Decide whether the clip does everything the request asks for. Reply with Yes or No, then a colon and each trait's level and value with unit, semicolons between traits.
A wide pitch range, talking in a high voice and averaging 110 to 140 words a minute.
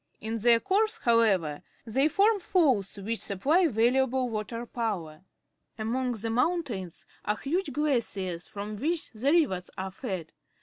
Yes: wide, 5.9 semitones; high, 230 Hz; slow, 135 wpm